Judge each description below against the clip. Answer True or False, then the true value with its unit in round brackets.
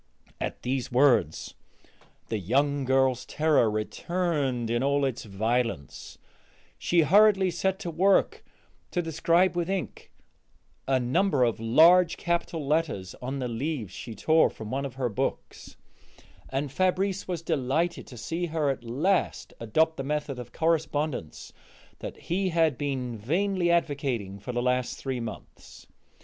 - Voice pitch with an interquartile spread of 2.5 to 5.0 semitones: False (5.5 semitones)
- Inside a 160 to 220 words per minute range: False (140 wpm)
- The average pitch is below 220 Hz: True (140 Hz)